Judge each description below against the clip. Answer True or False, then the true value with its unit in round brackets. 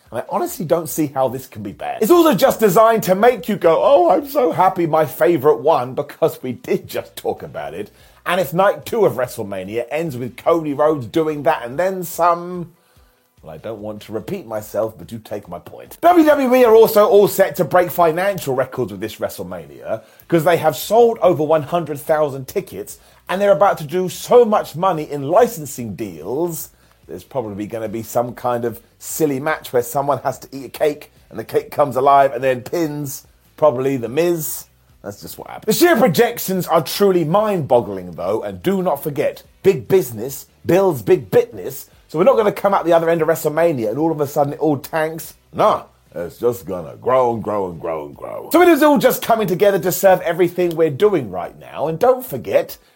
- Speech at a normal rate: False (210 wpm)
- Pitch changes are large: True (6.6 semitones)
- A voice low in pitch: False (165 Hz)